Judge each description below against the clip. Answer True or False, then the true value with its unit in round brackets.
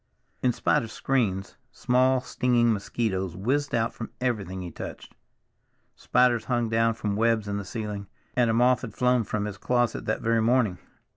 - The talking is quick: False (170 wpm)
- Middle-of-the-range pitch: False (115 Hz)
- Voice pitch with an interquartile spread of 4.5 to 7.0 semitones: False (3.2 semitones)